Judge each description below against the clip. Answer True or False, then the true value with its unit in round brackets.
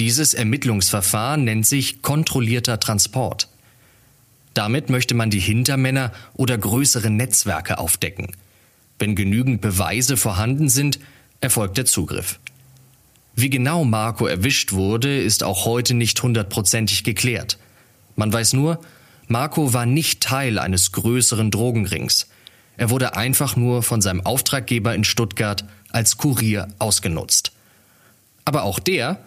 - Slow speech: True (120 wpm)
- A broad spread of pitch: False (3.5 semitones)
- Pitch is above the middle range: False (120 Hz)